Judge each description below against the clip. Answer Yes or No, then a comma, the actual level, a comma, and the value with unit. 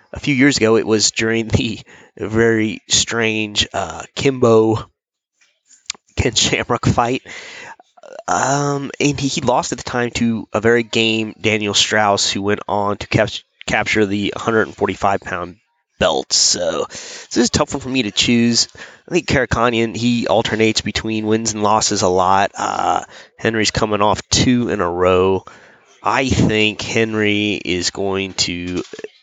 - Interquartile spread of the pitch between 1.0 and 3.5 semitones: Yes, average, 2.8 semitones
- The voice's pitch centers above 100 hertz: Yes, low, 110 Hz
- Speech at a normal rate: Yes, average, 150 wpm